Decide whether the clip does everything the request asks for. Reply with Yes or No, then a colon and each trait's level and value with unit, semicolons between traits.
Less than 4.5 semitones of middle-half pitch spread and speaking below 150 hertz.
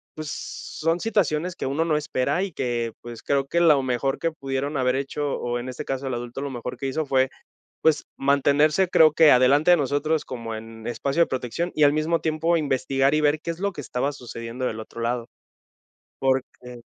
Yes: average, 3.6 semitones; medium, 140 Hz